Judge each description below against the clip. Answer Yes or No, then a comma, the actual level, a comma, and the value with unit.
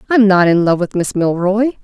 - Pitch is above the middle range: Yes, high, 195 Hz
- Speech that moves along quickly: Yes, fast, 230 wpm